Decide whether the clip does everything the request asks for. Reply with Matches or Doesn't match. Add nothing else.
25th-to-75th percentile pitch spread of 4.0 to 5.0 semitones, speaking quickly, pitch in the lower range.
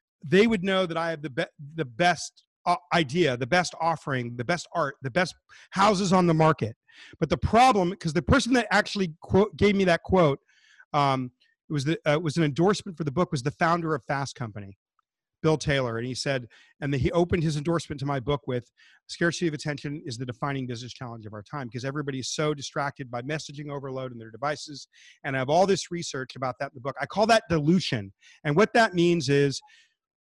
Doesn't match